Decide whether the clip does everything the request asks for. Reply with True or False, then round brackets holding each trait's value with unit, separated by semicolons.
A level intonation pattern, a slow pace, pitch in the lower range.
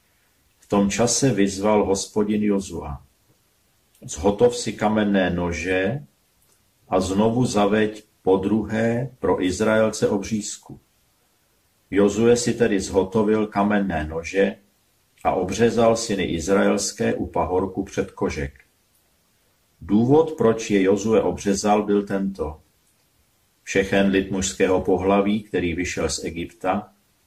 True (2.2 semitones; 105 wpm; 100 Hz)